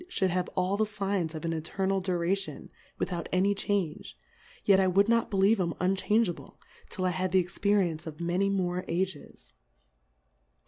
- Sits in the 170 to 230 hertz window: Yes, medium, 185 Hz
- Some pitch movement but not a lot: No, narrow, 2.2 semitones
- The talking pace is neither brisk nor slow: Yes, average, 170 wpm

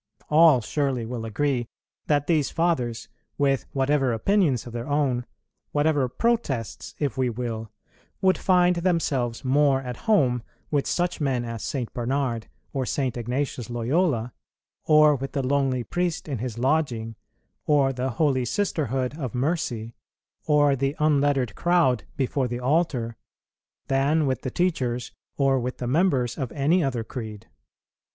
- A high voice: No, low, 135 Hz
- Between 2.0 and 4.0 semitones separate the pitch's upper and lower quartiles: Yes, average, 3.5 semitones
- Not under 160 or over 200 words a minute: No, average, 145 wpm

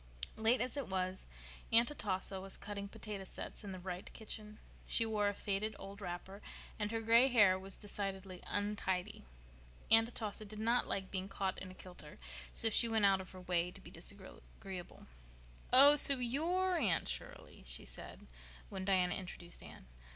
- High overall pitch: Yes, high, 200 Hz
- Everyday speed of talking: Yes, average, 175 wpm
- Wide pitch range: No, average, 3.1 semitones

